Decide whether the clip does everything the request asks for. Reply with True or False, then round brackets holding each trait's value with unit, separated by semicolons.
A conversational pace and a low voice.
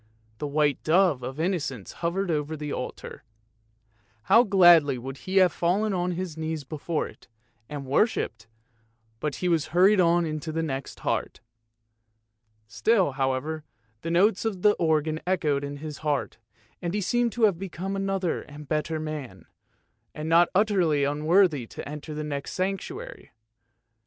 False (155 wpm; 160 Hz)